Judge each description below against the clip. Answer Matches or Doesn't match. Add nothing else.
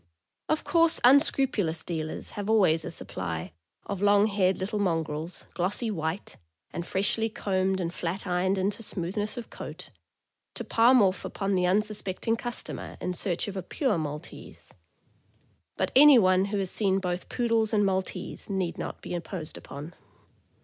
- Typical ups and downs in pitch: Matches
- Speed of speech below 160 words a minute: Matches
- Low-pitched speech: Doesn't match